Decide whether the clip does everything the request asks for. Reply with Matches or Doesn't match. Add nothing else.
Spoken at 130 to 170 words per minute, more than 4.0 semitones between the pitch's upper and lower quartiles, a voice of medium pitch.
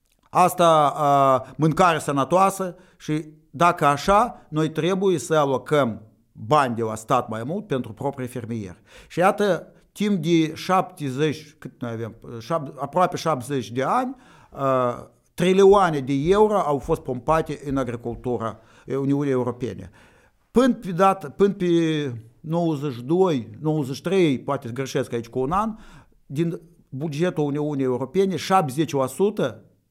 Doesn't match